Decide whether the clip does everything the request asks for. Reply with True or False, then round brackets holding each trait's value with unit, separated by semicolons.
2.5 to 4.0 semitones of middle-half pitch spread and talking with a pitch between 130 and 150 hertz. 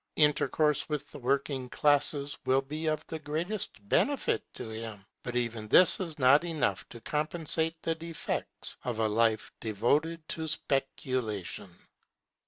False (5.3 semitones; 140 Hz)